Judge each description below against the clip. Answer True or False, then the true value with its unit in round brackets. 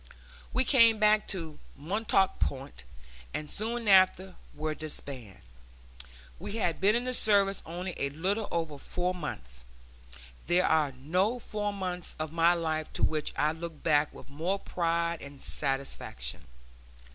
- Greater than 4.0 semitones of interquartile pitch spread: True (4.7 semitones)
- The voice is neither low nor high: True (170 Hz)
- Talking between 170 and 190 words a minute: False (145 wpm)